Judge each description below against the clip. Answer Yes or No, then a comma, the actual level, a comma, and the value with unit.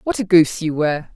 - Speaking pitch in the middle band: Yes, medium, 170 Hz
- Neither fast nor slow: No, fast, 260 wpm